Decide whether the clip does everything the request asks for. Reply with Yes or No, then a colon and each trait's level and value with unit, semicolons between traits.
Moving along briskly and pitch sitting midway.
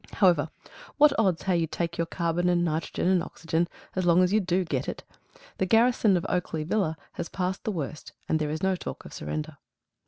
Yes: fast, 210 wpm; medium, 175 Hz